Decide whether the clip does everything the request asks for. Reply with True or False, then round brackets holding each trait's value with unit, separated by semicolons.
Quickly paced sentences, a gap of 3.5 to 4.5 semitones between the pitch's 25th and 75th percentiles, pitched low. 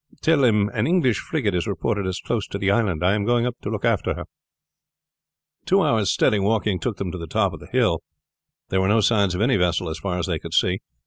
True (245 wpm; 4.0 semitones; 100 Hz)